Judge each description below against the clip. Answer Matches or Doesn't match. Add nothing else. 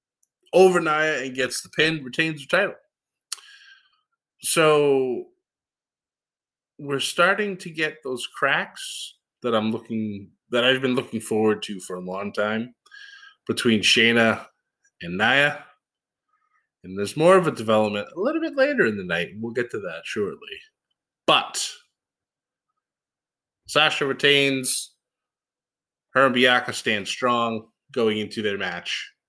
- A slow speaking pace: Matches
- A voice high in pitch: Doesn't match